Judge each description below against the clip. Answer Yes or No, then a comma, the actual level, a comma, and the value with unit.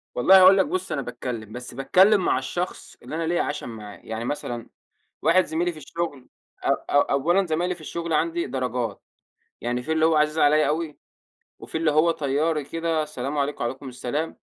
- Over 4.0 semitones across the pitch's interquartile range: Yes, average, 4.6 semitones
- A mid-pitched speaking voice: Yes, medium, 150 Hz